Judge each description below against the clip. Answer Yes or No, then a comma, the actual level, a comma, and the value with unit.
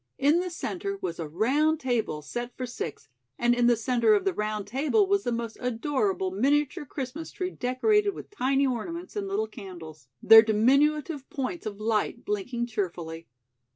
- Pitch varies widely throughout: Yes, wide, 6.5 semitones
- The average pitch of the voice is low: No, very high, 250 Hz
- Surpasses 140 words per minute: Yes, average, 170 wpm